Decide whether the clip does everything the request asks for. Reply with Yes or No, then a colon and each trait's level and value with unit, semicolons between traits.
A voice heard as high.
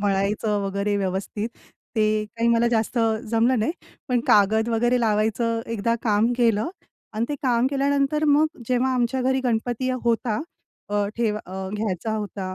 Yes: high, 225 Hz